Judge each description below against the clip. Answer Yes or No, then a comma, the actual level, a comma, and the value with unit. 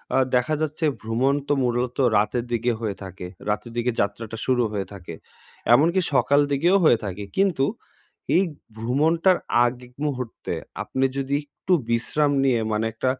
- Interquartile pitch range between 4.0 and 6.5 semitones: Yes, average, 4.3 semitones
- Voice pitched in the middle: No, low, 125 Hz